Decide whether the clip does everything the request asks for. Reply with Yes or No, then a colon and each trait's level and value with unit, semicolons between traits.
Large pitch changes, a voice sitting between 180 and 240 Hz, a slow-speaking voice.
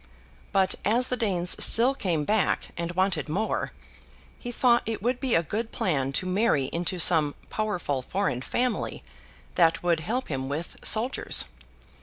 No: wide, 5.7 semitones; medium, 185 Hz; average, 155 wpm